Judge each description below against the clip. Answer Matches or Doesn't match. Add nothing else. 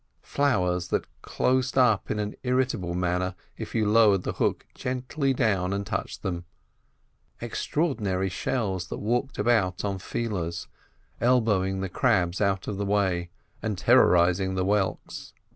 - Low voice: Matches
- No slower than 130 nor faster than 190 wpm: Matches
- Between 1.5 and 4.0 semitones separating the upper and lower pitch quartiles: Doesn't match